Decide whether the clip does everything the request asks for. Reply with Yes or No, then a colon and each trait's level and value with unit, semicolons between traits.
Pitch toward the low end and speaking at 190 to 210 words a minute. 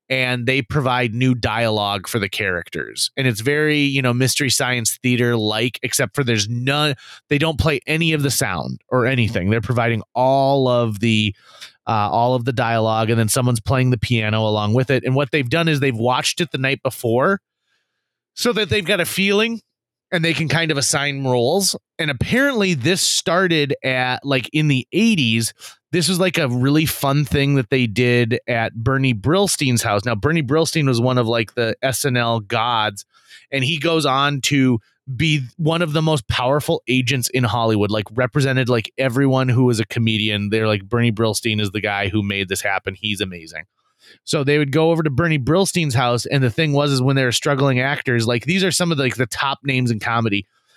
Yes: low, 130 Hz; fast, 205 wpm